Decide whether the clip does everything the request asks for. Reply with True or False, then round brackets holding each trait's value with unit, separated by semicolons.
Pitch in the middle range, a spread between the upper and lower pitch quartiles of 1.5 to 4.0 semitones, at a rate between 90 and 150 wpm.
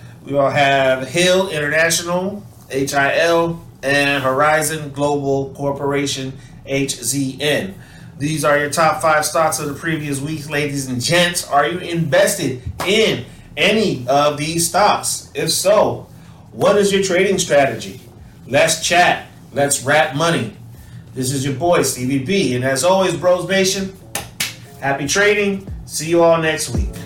True (145 Hz; 3.6 semitones; 140 wpm)